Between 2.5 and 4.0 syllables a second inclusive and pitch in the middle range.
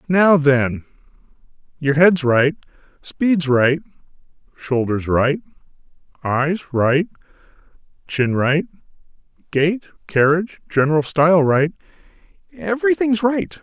Yes: 3.9 syllables/s; medium, 160 Hz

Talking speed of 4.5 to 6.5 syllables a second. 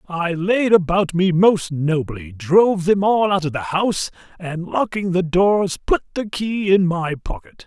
No: 4.1 syllables/s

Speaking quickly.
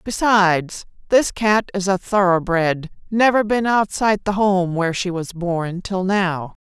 No: average, 155 wpm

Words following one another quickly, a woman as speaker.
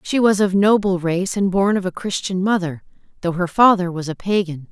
Yes: fast, 215 wpm; female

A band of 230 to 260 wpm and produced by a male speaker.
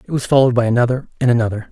Yes: fast, 245 wpm; male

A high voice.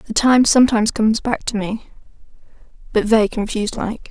Yes: high, 220 Hz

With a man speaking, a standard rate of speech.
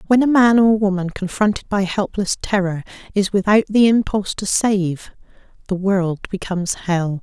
No: female; average, 160 wpm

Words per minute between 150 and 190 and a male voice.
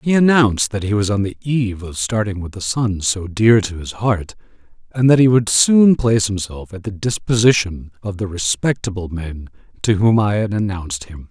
No: average, 200 wpm; male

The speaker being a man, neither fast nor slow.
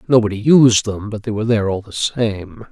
No: male; fast, 220 wpm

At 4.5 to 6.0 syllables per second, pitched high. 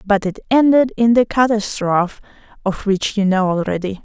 Yes: 5.1 syllables/s; high, 210 Hz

